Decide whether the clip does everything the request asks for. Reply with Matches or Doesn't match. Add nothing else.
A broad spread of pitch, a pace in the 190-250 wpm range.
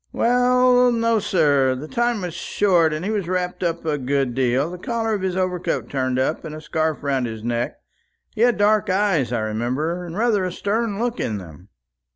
Matches